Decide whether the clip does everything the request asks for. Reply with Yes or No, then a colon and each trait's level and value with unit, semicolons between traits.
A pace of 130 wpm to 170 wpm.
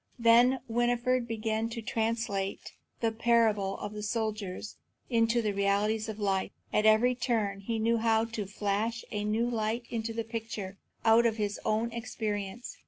Yes: average, 160 wpm